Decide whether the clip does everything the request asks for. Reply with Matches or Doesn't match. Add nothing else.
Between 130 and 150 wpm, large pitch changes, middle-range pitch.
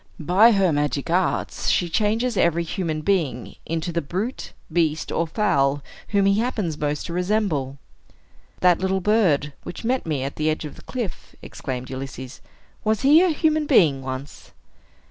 Doesn't match